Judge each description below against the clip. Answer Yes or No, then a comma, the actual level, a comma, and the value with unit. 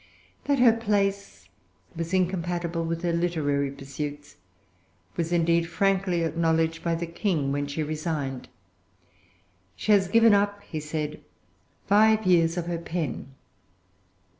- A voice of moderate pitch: Yes, medium, 170 Hz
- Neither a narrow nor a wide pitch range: Yes, average, 3.5 semitones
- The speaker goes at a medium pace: No, slow, 125 wpm